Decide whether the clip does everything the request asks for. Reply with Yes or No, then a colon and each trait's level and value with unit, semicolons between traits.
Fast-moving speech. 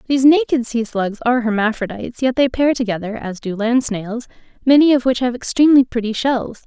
No: average, 190 wpm